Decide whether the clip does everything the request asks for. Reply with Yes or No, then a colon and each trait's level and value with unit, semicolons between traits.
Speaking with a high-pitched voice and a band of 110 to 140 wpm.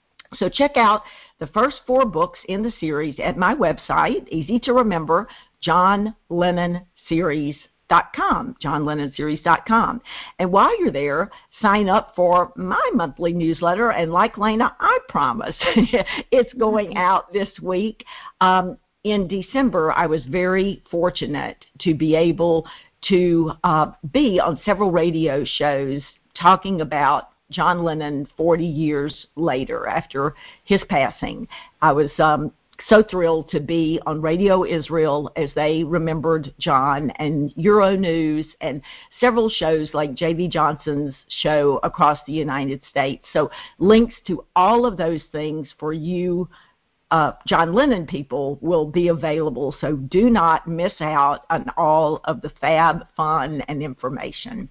No: medium, 165 Hz; slow, 135 wpm